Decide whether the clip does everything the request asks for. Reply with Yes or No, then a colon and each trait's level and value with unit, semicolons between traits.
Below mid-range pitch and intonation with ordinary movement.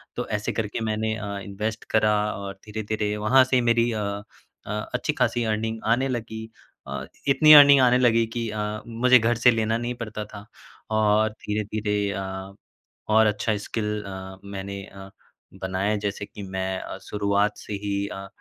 No: low, 110 Hz; narrow, 2.1 semitones